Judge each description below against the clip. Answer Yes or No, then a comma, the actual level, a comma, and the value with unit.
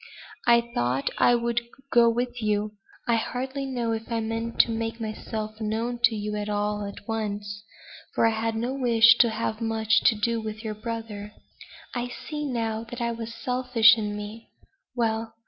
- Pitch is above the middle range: Yes, high, 225 Hz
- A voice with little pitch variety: Yes, narrow, 1.5 semitones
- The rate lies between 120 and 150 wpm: No, average, 175 wpm